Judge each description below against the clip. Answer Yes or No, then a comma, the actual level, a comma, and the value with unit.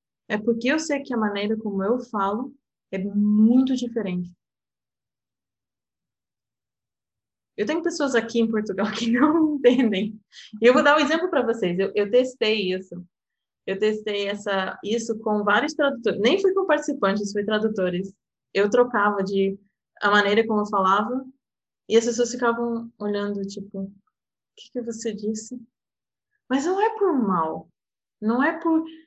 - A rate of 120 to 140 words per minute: No, average, 155 wpm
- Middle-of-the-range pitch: No, high, 220 Hz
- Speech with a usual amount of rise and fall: Yes, average, 4.2 semitones